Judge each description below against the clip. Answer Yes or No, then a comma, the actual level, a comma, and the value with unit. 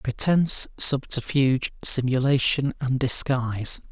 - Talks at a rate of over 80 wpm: No, slow, 75 wpm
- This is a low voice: Yes, low, 130 Hz